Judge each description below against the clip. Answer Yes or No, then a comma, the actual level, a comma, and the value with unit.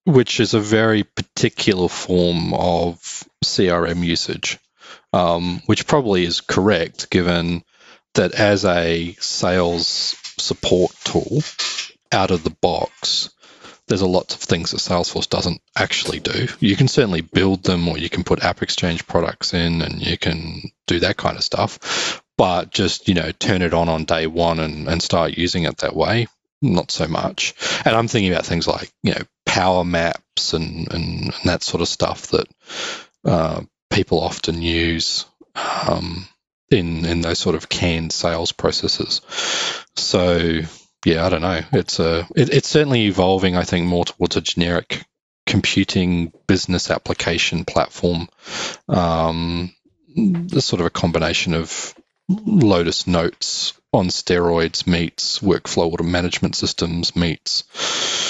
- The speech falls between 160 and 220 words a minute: No, average, 150 wpm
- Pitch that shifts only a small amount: Yes, narrow, 2.0 semitones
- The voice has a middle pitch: No, very low, 85 Hz